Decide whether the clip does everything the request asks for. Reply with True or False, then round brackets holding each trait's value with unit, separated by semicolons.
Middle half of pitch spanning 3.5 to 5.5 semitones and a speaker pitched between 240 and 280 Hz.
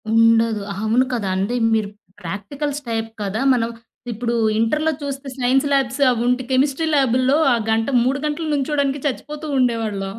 True (3.8 semitones; 250 Hz)